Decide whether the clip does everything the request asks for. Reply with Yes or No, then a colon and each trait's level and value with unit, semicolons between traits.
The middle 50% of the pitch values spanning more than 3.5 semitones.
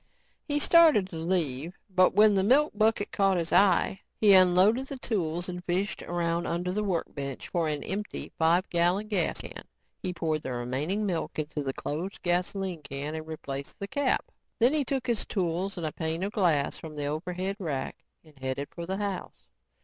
Yes: average, 4.1 semitones